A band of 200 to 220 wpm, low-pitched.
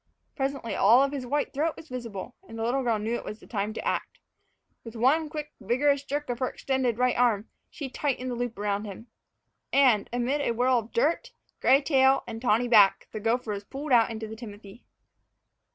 No: fast, 205 wpm; high, 245 Hz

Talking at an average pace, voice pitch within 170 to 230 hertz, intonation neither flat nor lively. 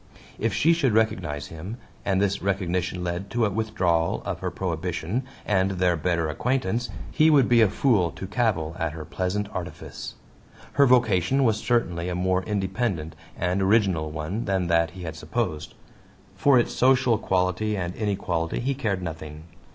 No: average, 165 wpm; very low, 95 Hz; average, 4.5 semitones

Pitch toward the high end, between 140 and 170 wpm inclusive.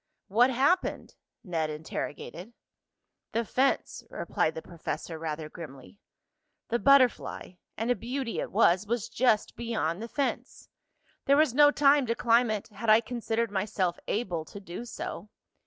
Yes: high, 225 Hz; average, 145 wpm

